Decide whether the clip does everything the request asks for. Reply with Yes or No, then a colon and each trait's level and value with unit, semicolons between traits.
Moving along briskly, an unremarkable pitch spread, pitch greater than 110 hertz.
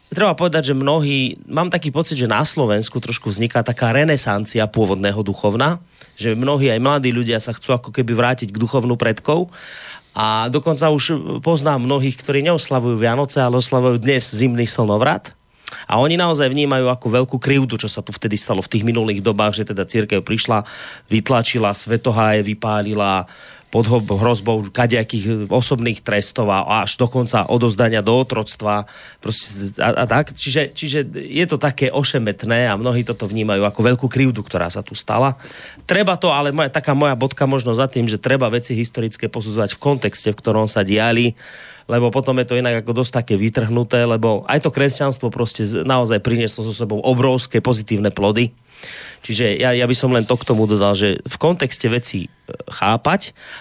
Yes: fast, 170 wpm; average, 3.7 semitones; low, 120 Hz